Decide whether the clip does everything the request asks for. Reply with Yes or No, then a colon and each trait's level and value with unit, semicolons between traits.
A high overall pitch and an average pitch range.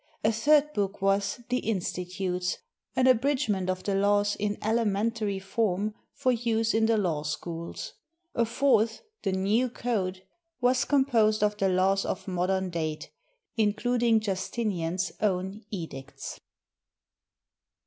Yes: high, 205 Hz; average, 3.5 semitones